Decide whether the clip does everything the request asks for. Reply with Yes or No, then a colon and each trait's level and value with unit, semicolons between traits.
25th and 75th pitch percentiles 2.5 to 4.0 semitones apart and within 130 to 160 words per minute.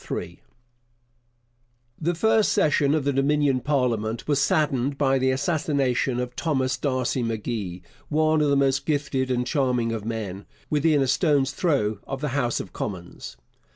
Yes: average, 3.4 semitones; average, 150 wpm